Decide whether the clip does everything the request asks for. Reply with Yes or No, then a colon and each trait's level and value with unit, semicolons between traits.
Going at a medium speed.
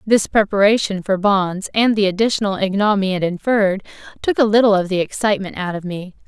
Yes: average, 180 wpm